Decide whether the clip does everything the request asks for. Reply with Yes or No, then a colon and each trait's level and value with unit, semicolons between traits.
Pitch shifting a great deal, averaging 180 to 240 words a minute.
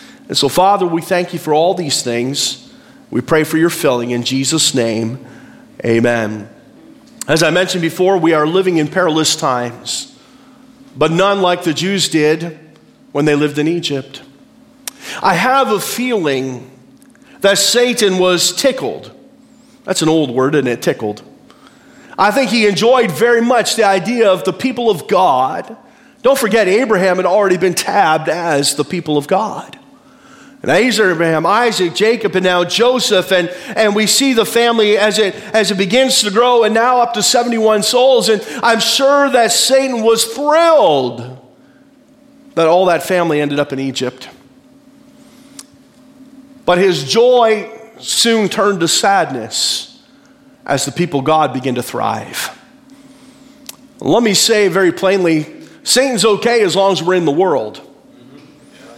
No: wide, 8.1 semitones; average, 155 wpm